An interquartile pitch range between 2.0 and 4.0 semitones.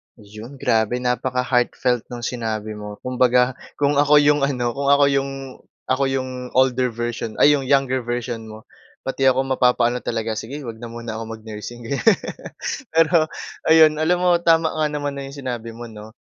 Yes: average, 3.3 semitones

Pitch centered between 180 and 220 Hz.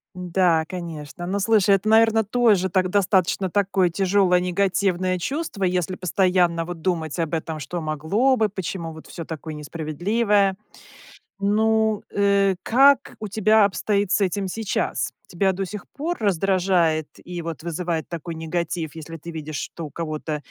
Yes: medium, 185 Hz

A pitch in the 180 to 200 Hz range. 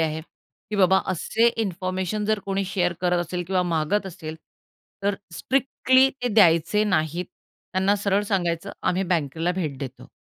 Yes: medium, 185 Hz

